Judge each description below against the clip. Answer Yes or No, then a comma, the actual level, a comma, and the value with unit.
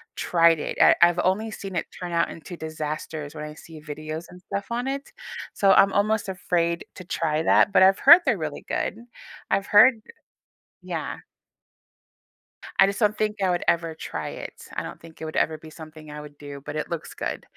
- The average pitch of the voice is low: No, medium, 170 Hz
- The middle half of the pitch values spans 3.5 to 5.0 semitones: Yes, average, 4.2 semitones